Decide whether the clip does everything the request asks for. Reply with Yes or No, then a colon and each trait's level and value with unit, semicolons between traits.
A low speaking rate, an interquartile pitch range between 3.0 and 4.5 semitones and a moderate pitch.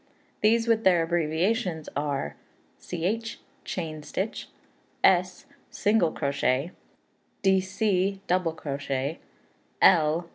Yes: slow, 85 wpm; average, 4.0 semitones; medium, 175 Hz